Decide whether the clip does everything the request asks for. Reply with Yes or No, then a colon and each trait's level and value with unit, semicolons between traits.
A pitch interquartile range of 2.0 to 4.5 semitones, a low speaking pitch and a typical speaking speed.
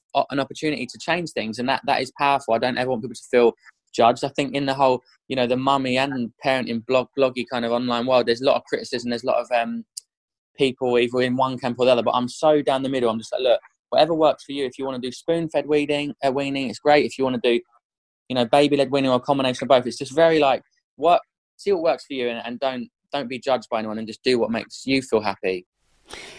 No: narrow, 2.4 semitones; low, 130 Hz; fast, 270 wpm